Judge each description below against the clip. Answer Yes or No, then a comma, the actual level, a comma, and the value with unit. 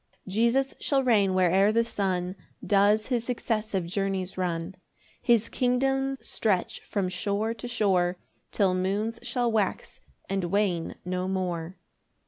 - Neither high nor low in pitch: No, high, 200 Hz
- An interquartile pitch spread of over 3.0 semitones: Yes, average, 3.8 semitones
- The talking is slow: Yes, slow, 130 wpm